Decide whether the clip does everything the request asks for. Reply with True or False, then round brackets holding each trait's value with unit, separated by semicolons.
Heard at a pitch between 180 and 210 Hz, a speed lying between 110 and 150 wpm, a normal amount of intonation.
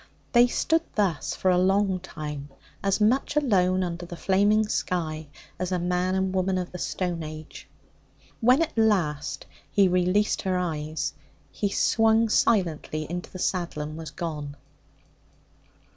True (185 Hz; 145 wpm; 3.7 semitones)